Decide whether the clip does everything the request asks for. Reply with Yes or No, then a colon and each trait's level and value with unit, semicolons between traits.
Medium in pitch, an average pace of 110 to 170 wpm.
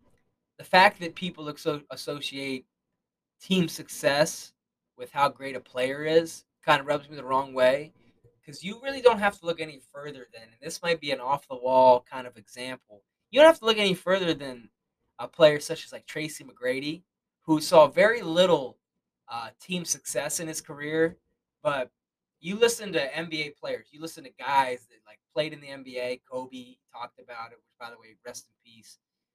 No: medium, 150 Hz; average, 185 wpm